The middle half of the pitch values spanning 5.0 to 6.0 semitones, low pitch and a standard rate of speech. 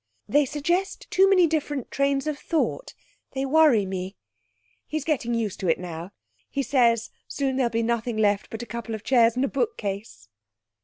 No: average, 5.3 semitones; very high, 250 Hz; average, 175 wpm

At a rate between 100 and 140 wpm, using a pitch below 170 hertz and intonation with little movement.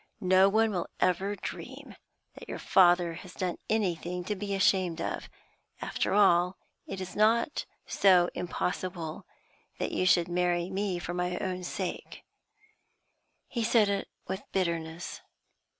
No: slow, 135 wpm; medium, 185 Hz; narrow, 2.0 semitones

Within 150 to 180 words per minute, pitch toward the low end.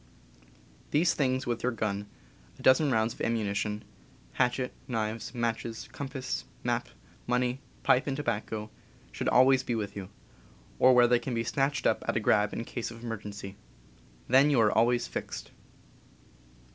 Yes: average, 160 wpm; low, 120 Hz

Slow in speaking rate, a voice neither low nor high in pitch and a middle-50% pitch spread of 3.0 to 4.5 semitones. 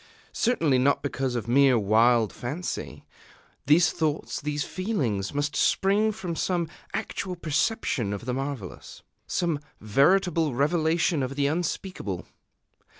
No: slow, 120 wpm; medium, 145 Hz; wide, 5.6 semitones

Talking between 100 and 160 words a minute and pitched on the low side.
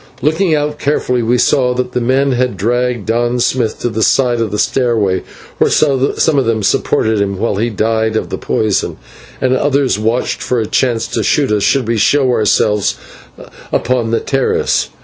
No: average, 185 wpm; low, 120 Hz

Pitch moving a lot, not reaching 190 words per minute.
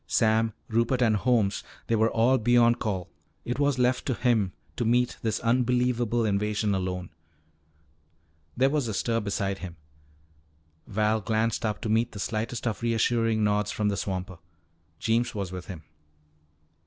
No: narrow, 2.6 semitones; average, 150 wpm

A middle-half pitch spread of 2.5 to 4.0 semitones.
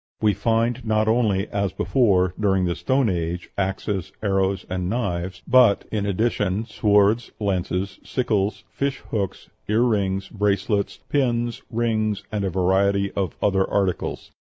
Yes: average, 2.8 semitones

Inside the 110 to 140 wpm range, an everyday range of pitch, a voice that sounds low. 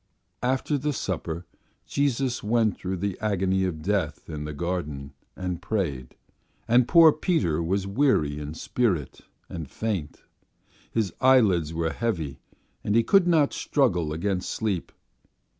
No: slow, 135 wpm; wide, 6.7 semitones; very low, 95 Hz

